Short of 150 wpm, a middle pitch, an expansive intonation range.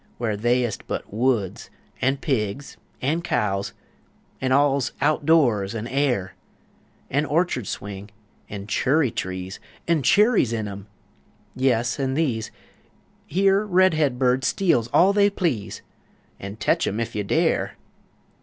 No: slow, 135 wpm; low, 125 Hz; wide, 6.3 semitones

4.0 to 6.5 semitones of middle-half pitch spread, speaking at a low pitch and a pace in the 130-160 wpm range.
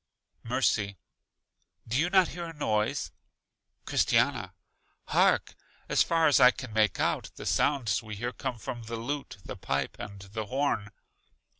Yes: average, 5.0 semitones; low, 120 Hz; average, 150 wpm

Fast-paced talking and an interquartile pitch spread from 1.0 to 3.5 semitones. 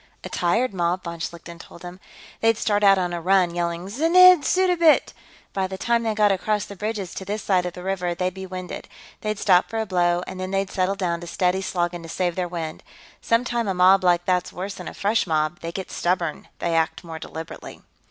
Yes: fast, 220 wpm; average, 2.8 semitones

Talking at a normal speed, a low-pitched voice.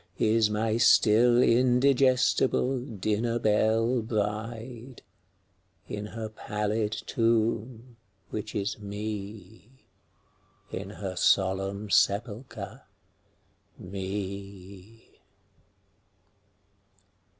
No: slow, 65 wpm; low, 110 Hz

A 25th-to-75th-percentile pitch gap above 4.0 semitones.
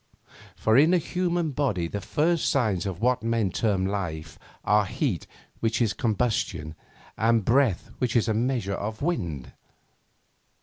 Yes: average, 5.1 semitones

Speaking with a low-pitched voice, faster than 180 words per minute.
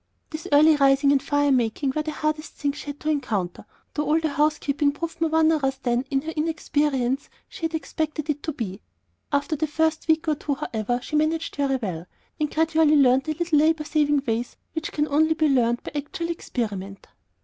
No: very high, 295 Hz; average, 200 wpm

